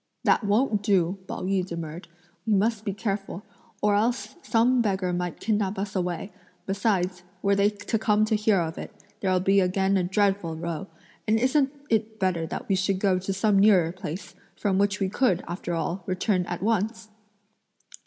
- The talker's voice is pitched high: Yes, high, 195 Hz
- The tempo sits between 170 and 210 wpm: Yes, average, 180 wpm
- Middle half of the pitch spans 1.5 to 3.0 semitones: Yes, narrow, 2.6 semitones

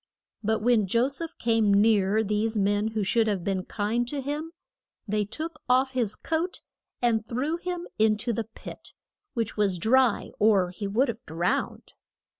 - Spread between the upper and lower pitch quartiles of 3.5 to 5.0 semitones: Yes, average, 3.8 semitones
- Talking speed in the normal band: Yes, average, 170 wpm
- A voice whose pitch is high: Yes, high, 220 Hz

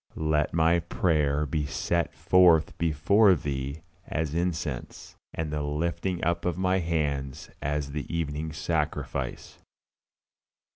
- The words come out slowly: Yes, slow, 115 wpm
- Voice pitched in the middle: No, very low, 80 Hz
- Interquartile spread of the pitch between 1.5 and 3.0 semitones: Yes, narrow, 2.6 semitones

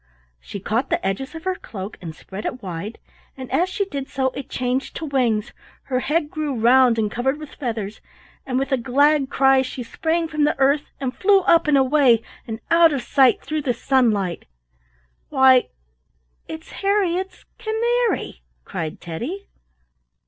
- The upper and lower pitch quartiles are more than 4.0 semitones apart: Yes, average, 4.8 semitones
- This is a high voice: Yes, very high, 265 Hz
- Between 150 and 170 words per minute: Yes, average, 165 wpm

